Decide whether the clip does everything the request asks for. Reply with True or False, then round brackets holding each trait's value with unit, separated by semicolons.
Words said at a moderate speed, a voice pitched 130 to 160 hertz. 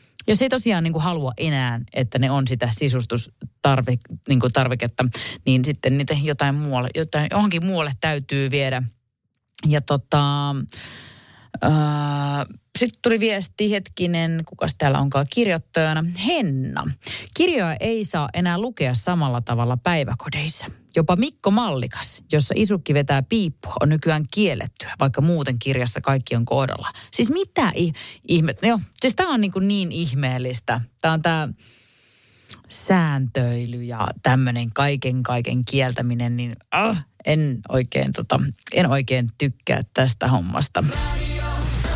True (130 wpm; 140 Hz)